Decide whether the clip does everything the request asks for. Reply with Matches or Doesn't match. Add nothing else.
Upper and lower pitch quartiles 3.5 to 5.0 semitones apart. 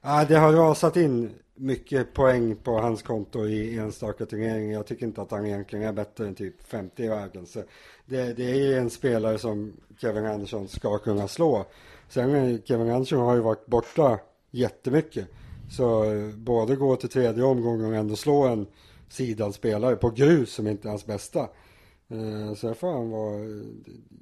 Doesn't match